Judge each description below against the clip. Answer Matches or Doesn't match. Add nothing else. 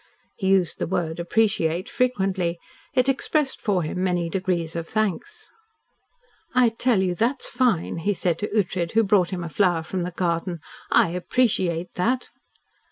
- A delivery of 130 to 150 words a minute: Doesn't match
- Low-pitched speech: Doesn't match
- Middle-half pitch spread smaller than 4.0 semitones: Doesn't match